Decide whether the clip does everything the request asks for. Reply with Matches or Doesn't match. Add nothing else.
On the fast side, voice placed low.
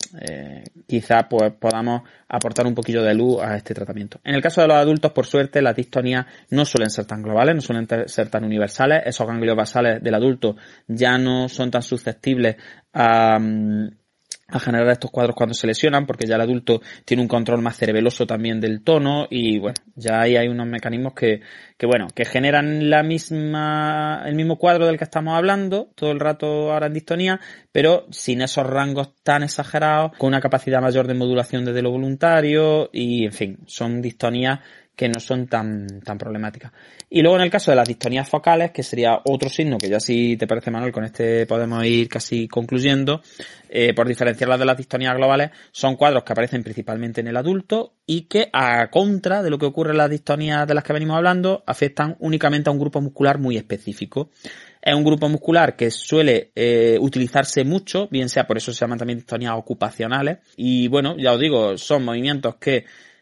Matches